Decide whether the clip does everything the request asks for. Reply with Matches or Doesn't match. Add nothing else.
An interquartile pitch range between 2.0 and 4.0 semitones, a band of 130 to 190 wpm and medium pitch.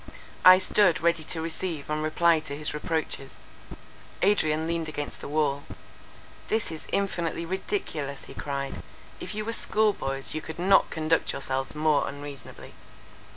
Matches